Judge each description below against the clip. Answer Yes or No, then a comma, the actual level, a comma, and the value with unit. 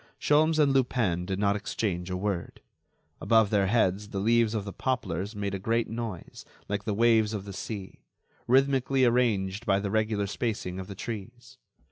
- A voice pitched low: Yes, low, 105 Hz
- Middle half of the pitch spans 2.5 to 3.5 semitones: Yes, average, 3.2 semitones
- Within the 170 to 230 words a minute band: Yes, average, 175 wpm